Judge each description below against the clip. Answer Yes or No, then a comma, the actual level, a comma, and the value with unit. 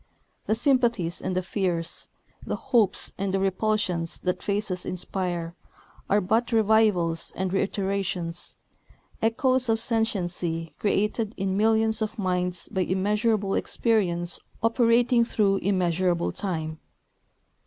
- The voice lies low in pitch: No, high, 195 Hz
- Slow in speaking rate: Yes, slow, 110 wpm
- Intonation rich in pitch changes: No, average, 3.6 semitones